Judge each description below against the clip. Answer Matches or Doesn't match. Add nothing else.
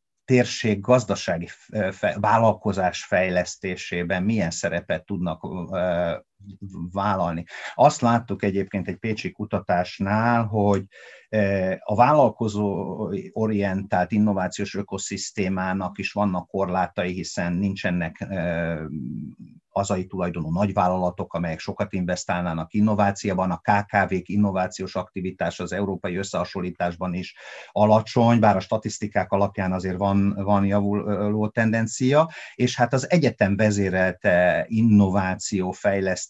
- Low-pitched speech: Matches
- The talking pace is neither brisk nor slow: Doesn't match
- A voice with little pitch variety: Matches